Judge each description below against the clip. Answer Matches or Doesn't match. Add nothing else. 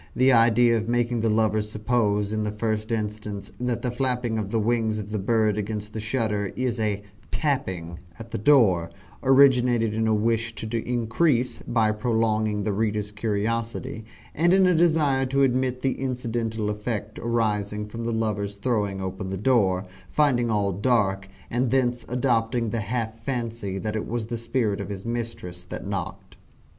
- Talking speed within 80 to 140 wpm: Doesn't match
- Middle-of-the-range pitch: Doesn't match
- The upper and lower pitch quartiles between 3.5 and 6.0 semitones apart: Doesn't match